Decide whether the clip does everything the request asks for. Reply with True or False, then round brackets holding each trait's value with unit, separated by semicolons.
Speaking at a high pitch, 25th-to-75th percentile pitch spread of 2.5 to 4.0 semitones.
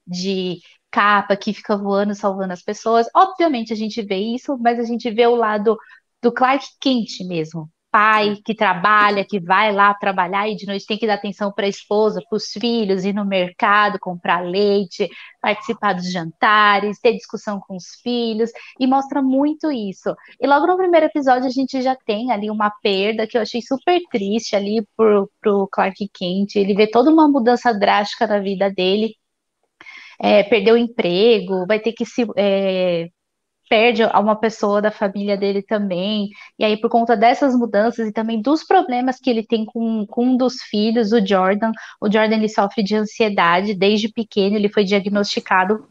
True (215 Hz; 2.8 semitones)